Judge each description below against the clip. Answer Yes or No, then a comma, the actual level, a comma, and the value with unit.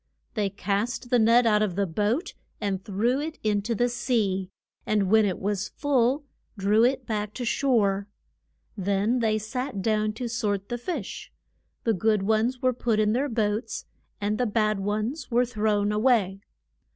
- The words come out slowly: No, average, 175 wpm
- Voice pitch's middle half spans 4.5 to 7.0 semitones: No, average, 3.0 semitones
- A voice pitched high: Yes, high, 215 Hz